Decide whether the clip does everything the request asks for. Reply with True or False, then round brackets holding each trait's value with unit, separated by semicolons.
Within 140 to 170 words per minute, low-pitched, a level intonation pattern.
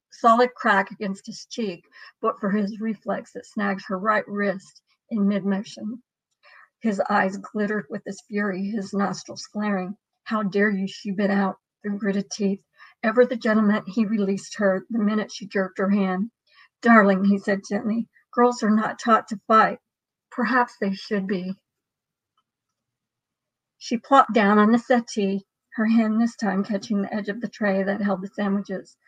False (165 wpm; 205 Hz; 2.0 semitones)